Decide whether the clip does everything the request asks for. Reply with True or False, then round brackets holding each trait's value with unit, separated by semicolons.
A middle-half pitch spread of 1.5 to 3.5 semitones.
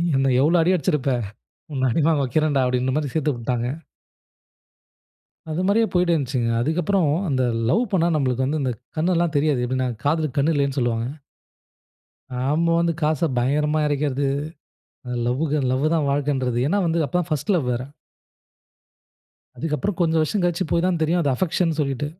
False (3.9 semitones)